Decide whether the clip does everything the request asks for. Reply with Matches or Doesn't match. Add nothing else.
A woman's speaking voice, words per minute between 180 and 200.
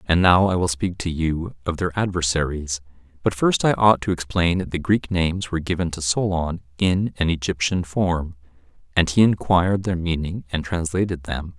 Doesn't match